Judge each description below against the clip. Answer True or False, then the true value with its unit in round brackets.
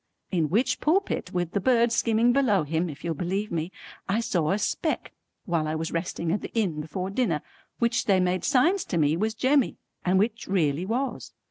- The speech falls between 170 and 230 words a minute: True (200 wpm)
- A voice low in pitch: False (190 Hz)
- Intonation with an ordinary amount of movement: False (5.9 semitones)